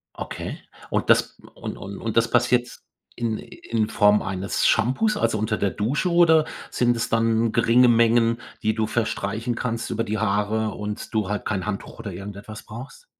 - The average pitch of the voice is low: Yes, low, 115 Hz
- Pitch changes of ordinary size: No, narrow, 2.3 semitones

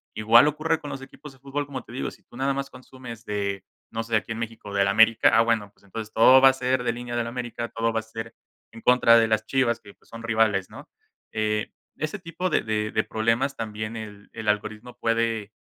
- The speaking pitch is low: Yes, low, 115 Hz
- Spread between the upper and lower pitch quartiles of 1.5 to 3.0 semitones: Yes, average, 2.7 semitones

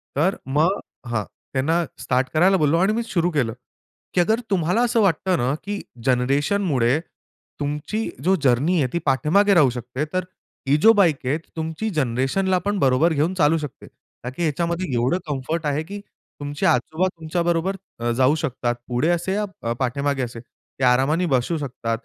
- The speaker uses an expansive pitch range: Yes, wide, 5.8 semitones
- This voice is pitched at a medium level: Yes, medium, 155 Hz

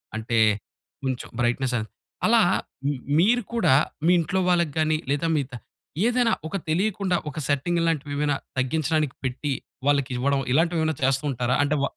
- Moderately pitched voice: Yes, medium, 145 Hz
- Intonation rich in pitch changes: No, average, 4.1 semitones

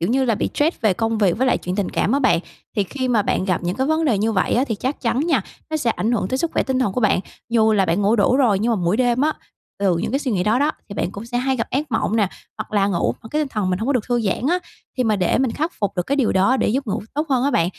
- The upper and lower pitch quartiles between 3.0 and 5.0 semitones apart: Yes, average, 4.6 semitones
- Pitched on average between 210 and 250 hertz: Yes, high, 230 Hz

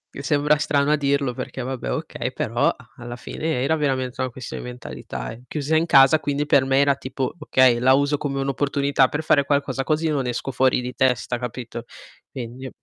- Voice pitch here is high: No, low, 135 Hz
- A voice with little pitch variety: Yes, narrow, 2.2 semitones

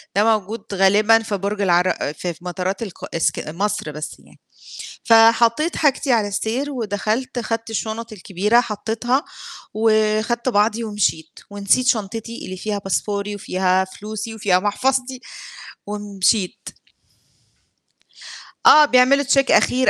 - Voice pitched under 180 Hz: No, high, 215 Hz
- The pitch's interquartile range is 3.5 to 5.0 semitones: No, average, 2.9 semitones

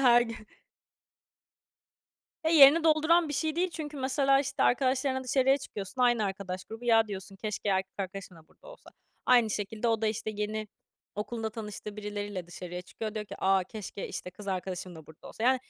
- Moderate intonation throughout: Yes, average, 5.0 semitones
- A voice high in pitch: Yes, high, 220 Hz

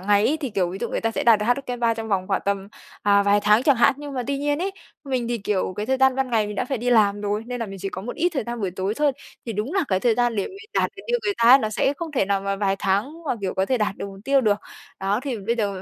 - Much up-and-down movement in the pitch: No, average, 4.7 semitones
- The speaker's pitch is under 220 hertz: No, high, 225 Hz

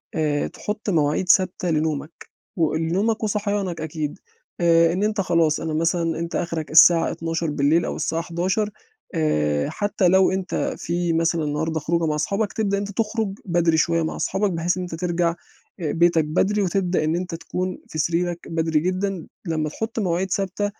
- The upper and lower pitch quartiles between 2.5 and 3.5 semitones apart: Yes, average, 2.9 semitones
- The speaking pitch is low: No, medium, 170 Hz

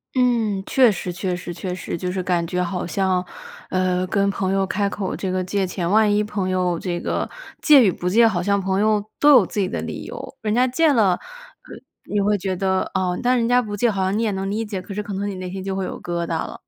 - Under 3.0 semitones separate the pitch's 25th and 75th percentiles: Yes, narrow, 2.5 semitones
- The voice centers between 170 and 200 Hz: Yes, high, 195 Hz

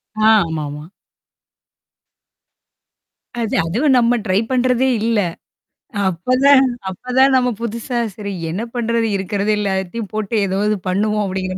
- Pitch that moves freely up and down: No, average, 4.3 semitones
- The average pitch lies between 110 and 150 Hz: No, high, 215 Hz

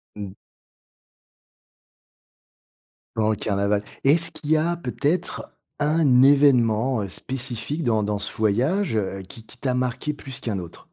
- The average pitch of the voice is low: Yes, low, 125 Hz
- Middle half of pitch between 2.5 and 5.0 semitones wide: No, wide, 5.5 semitones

